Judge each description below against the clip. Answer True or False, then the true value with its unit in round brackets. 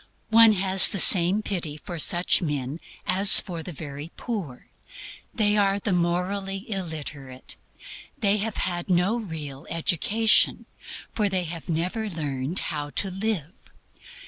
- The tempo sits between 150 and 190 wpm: False (135 wpm)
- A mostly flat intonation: False (4.2 semitones)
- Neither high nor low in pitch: True (180 Hz)